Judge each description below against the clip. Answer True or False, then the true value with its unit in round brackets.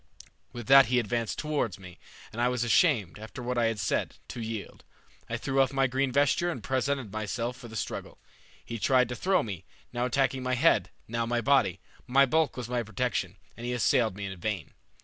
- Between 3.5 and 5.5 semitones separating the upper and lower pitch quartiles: False (3.1 semitones)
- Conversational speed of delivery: False (210 wpm)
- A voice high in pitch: False (120 Hz)